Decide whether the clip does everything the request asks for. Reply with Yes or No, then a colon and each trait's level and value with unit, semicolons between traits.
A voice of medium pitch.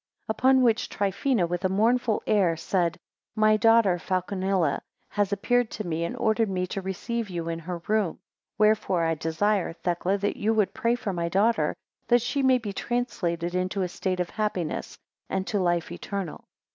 No: high, 195 Hz